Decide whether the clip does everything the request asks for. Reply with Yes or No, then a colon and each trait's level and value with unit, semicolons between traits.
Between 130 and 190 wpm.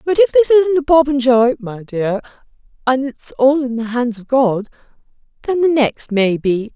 Yes: average, 170 wpm